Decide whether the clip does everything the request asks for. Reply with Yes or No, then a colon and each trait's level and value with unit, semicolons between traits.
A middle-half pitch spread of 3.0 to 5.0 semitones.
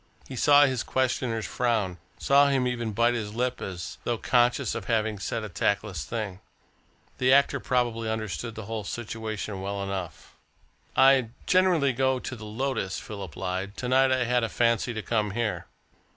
Yes: average, 3.6 semitones